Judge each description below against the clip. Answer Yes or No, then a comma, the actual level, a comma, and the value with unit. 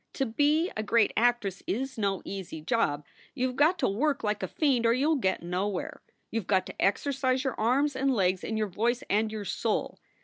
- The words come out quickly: Yes, fast, 225 wpm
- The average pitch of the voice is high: Yes, high, 230 Hz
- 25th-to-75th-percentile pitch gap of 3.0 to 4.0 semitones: No, average, 5.1 semitones